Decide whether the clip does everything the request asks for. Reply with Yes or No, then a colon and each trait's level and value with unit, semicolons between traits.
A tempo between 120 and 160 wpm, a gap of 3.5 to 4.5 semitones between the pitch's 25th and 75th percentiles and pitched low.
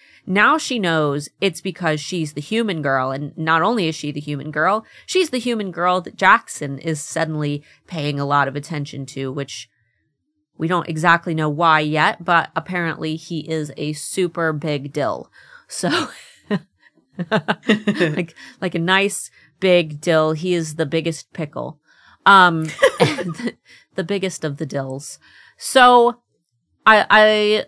No: average, 145 wpm; average, 4.2 semitones; medium, 165 Hz